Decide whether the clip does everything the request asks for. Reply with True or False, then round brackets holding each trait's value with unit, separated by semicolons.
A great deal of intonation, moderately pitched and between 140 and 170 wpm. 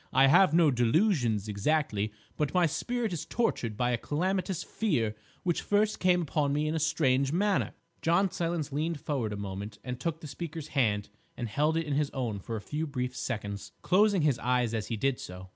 False (6.2 semitones; 145 Hz; 200 wpm)